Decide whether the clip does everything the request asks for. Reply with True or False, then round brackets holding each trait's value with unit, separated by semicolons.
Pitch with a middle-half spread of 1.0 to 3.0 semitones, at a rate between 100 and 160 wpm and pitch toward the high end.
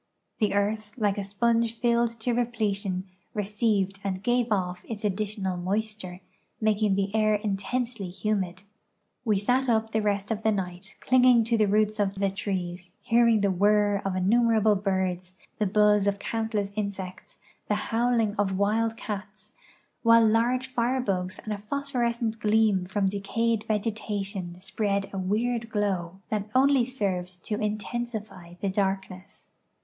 True (2.6 semitones; 150 wpm; 210 Hz)